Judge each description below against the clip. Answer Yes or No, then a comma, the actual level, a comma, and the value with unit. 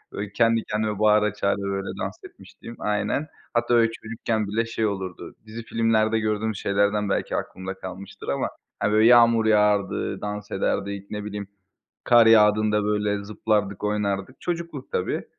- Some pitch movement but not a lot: No, narrow, 1.8 semitones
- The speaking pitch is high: No, low, 105 Hz